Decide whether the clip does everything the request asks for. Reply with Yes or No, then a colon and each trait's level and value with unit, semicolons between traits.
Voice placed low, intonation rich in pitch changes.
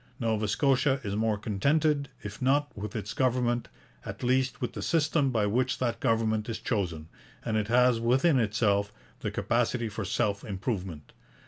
No: low, 115 Hz; average, 3.7 semitones